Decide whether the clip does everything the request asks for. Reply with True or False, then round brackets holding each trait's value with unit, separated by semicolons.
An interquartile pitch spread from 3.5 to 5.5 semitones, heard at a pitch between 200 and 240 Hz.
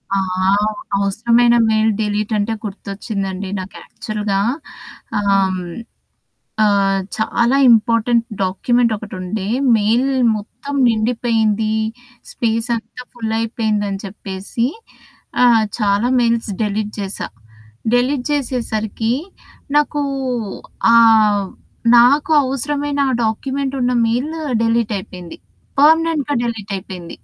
False (3.0 semitones; 225 Hz)